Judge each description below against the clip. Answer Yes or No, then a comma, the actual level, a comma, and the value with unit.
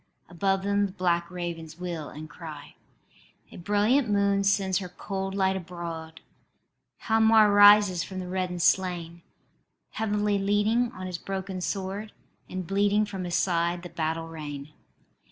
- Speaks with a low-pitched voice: No, medium, 185 Hz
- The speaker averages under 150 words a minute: Yes, average, 140 wpm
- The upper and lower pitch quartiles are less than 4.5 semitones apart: Yes, average, 2.9 semitones